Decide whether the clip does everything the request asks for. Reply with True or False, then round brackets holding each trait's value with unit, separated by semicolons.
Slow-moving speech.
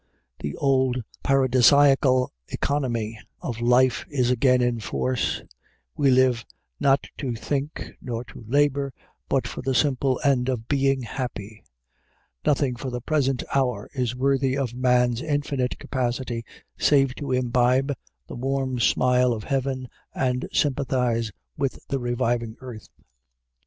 True (130 wpm)